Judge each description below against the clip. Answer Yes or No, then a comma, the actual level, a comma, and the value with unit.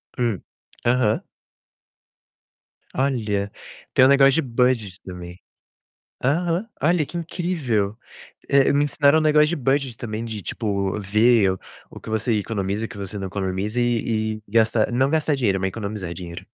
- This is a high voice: No, low, 115 Hz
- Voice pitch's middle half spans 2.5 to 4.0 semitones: No, wide, 5.4 semitones